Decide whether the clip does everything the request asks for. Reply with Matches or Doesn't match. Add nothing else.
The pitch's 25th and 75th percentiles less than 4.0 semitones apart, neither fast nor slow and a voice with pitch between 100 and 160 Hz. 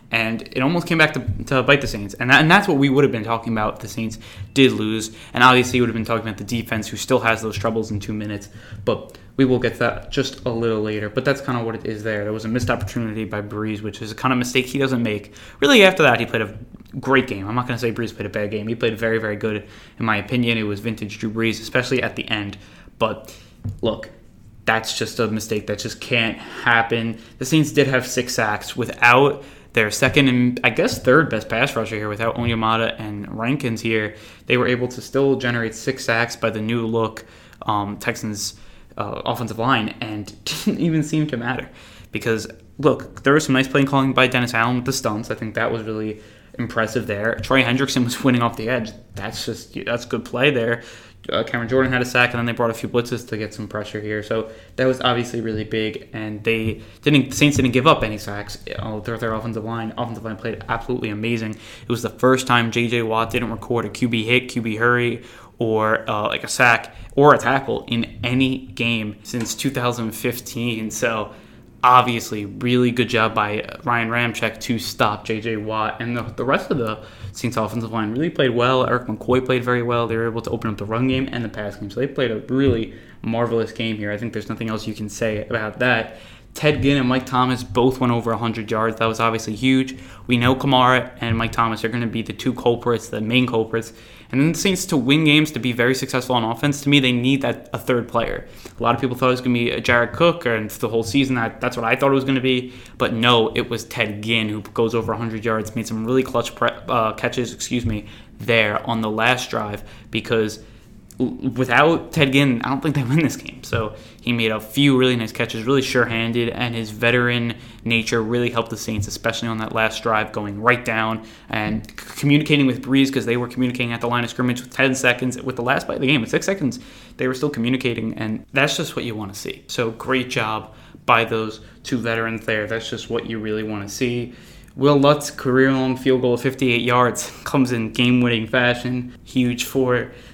Doesn't match